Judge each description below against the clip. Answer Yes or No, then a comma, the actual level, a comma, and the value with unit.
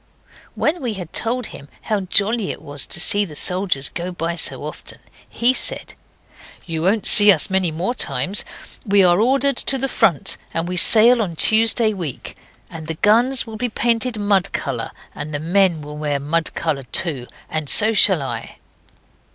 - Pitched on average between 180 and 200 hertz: Yes, high, 190 Hz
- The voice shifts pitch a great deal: Yes, wide, 5.8 semitones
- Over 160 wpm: Yes, average, 175 wpm